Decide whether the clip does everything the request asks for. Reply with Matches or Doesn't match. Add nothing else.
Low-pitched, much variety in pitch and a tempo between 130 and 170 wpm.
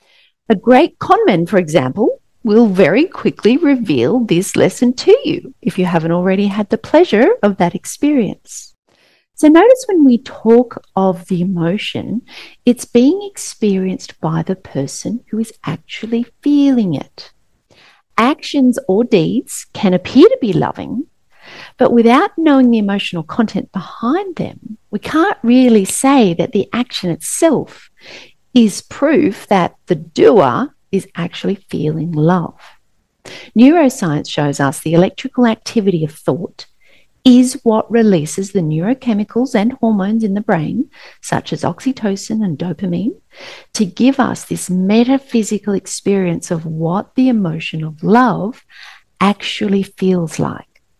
Doesn't match